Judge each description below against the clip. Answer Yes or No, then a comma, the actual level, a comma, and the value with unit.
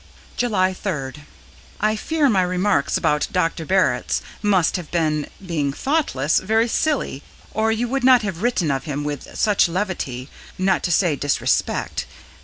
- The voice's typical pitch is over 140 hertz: Yes, medium, 185 Hz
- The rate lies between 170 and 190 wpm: No, average, 150 wpm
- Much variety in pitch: Yes, wide, 6.4 semitones